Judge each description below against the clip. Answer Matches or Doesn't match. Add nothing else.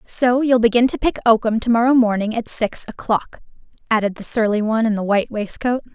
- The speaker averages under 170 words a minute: Doesn't match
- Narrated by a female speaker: Matches